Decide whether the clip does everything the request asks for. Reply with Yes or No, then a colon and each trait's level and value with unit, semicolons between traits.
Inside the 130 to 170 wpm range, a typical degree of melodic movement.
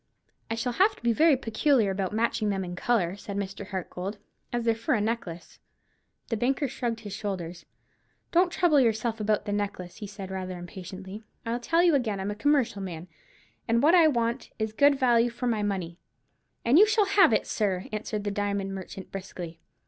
No: average, 195 wpm; average, 4.0 semitones